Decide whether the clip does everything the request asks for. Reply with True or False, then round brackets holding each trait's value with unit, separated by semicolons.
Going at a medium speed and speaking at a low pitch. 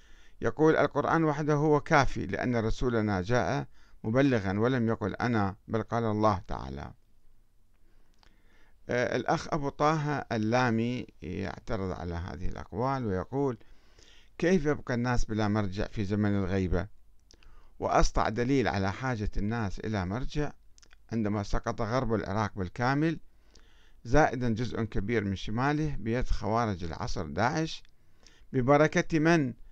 True (115 wpm; 115 Hz)